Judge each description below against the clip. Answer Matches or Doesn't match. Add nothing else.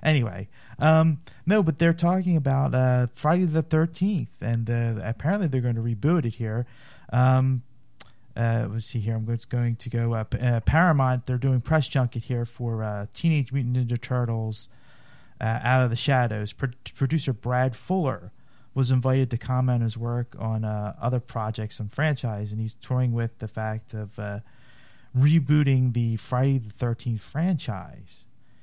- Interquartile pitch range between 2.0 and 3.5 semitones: Matches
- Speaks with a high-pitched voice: Doesn't match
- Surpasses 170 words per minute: Doesn't match